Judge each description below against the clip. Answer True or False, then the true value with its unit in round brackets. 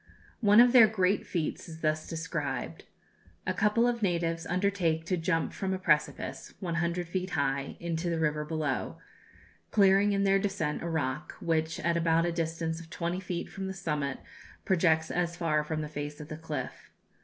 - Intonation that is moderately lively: True (3.2 semitones)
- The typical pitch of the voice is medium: True (165 Hz)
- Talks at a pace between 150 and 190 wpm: True (180 wpm)